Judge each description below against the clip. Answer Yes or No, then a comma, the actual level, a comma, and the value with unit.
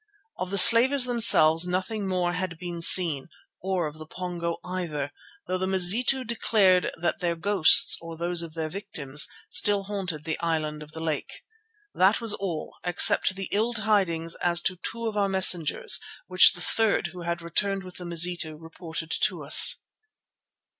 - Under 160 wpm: No, average, 165 wpm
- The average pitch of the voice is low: No, medium, 180 Hz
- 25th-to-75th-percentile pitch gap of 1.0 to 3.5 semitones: Yes, average, 3.1 semitones